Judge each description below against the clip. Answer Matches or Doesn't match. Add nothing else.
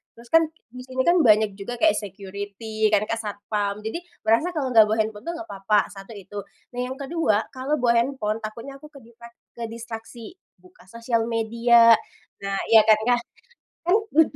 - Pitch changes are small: Doesn't match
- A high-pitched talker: Matches